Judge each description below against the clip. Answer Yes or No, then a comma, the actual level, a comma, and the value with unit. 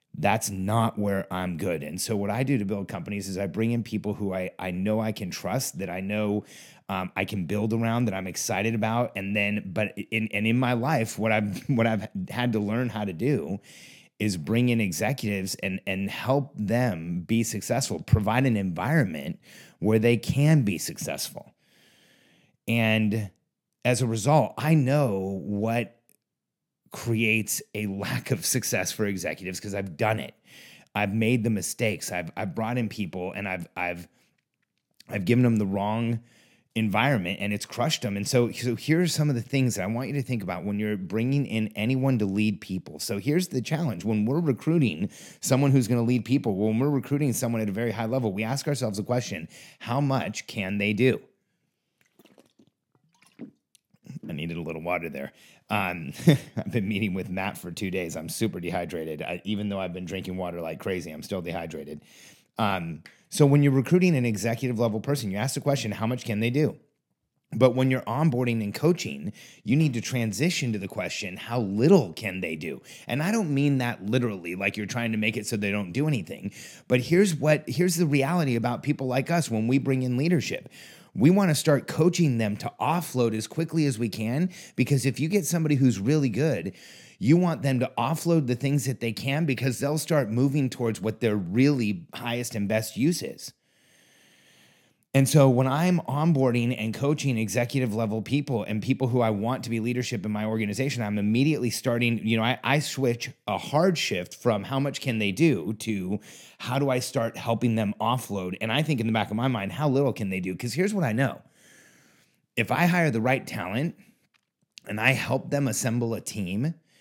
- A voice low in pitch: Yes, low, 115 Hz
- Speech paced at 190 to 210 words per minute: Yes, average, 200 wpm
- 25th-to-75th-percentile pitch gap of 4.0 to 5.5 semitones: Yes, average, 4.6 semitones